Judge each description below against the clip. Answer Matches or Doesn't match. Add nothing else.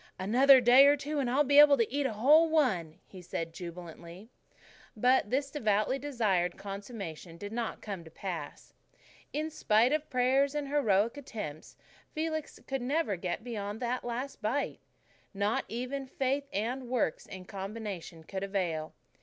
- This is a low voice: Doesn't match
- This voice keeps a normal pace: Matches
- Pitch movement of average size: Doesn't match